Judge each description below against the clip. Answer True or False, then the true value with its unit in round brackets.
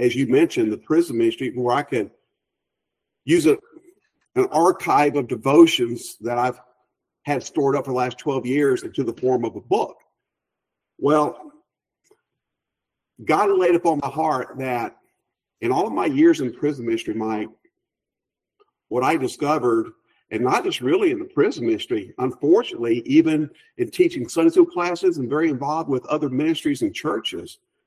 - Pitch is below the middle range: False (325 Hz)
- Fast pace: False (155 wpm)